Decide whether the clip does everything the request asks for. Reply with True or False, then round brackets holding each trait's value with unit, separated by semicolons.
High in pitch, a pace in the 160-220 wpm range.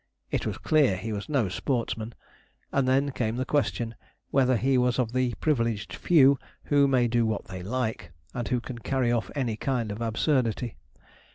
False (125 Hz; 180 wpm)